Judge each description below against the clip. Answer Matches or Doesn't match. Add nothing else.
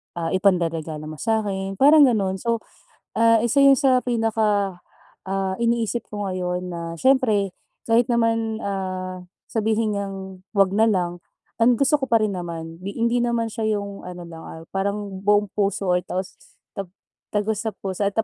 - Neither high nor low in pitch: Doesn't match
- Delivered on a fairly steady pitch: Doesn't match